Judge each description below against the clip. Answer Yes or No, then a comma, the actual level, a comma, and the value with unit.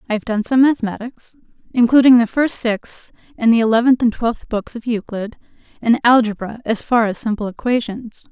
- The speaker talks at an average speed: Yes, average, 175 wpm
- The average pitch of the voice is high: Yes, high, 230 Hz